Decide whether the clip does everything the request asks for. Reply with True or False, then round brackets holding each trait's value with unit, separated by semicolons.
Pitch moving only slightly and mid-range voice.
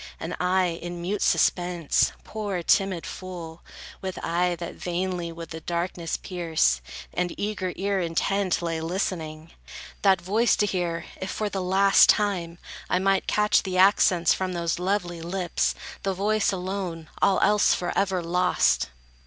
True (2.3 semitones; 180 Hz)